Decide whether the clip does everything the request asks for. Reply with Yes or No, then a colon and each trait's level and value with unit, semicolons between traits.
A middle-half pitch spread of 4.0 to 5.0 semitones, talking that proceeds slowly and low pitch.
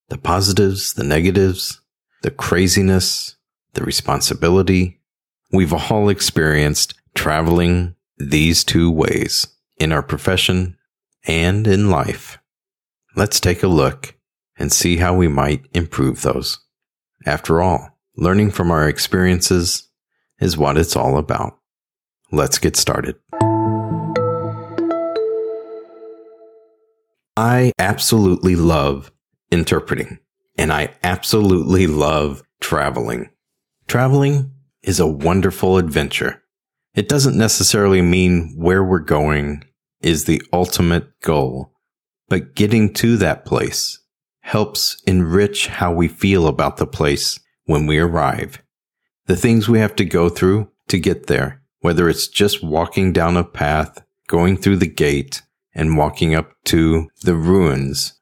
Yes: average, 4.3 semitones; slow, 115 wpm; very low, 90 Hz